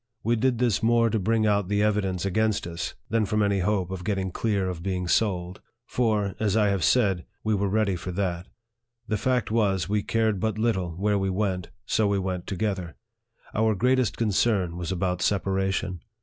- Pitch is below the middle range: Yes, low, 100 Hz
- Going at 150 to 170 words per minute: No, average, 190 wpm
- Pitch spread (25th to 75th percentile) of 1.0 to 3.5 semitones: Yes, average, 2.8 semitones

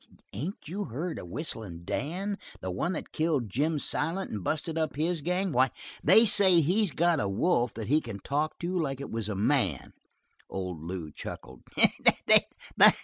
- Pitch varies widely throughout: Yes, wide, 8.6 semitones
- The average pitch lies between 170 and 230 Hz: No, medium, 150 Hz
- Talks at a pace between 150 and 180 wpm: Yes, average, 170 wpm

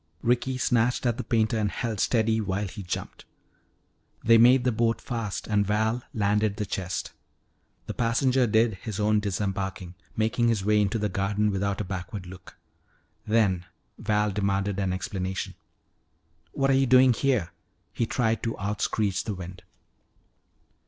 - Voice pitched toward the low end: Yes, low, 105 Hz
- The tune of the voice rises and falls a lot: No, average, 2.8 semitones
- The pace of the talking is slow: No, average, 155 wpm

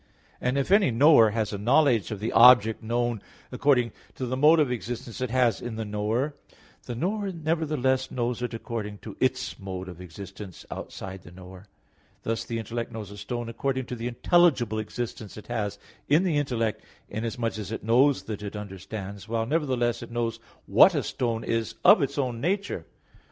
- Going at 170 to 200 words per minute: Yes, average, 185 wpm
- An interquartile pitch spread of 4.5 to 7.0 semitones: No, average, 3.4 semitones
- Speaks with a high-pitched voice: No, low, 115 Hz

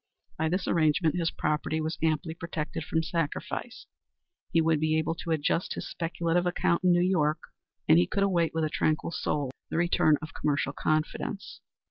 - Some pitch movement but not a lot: No, narrow, 1.7 semitones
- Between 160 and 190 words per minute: Yes, average, 175 wpm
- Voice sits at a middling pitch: Yes, medium, 160 Hz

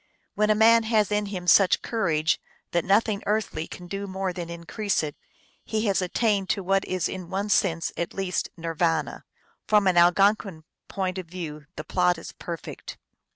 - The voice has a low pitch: No, high, 190 Hz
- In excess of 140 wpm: Yes, average, 185 wpm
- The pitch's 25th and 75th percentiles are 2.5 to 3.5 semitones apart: Yes, average, 3.2 semitones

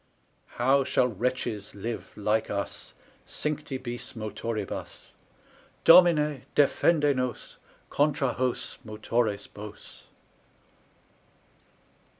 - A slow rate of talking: Yes, slow, 80 wpm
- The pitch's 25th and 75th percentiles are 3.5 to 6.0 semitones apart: Yes, average, 4.6 semitones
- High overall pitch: No, low, 125 Hz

